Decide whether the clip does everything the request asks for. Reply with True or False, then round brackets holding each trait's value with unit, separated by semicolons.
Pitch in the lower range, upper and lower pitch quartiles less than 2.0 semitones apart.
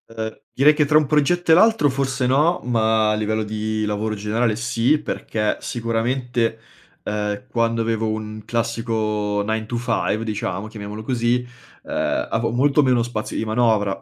False (115 Hz; 2.4 semitones)